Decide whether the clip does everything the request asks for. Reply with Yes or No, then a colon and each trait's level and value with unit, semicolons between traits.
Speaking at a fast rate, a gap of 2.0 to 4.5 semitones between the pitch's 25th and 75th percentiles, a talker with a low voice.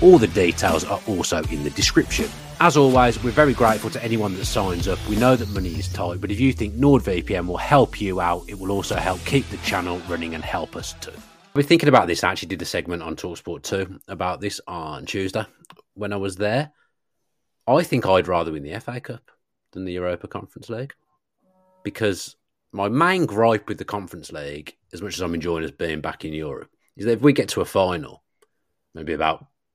No: fast, 215 wpm; wide, 5.4 semitones; low, 105 Hz